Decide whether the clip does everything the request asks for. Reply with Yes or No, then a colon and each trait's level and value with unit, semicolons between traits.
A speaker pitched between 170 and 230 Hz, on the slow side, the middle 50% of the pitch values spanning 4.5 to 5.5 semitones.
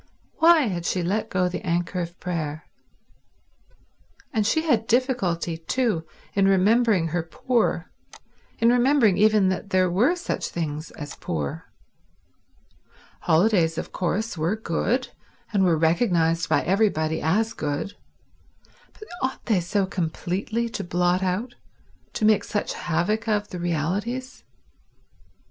Yes: high, 190 Hz; slow, 130 wpm; average, 4.8 semitones